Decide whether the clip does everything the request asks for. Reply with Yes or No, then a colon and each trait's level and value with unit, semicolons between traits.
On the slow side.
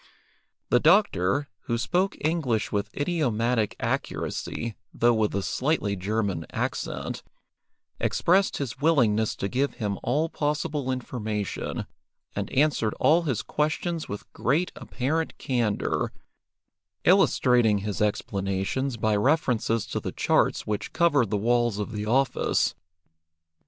Yes: slow, 120 wpm